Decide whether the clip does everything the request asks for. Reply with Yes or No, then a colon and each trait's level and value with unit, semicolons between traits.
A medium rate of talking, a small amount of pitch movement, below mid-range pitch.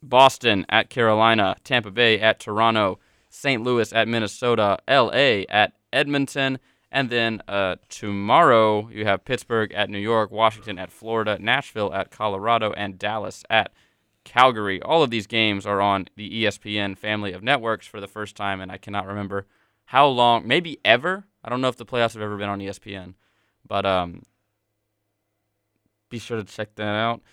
Yes: average, 165 wpm; narrow, 2.2 semitones; low, 105 Hz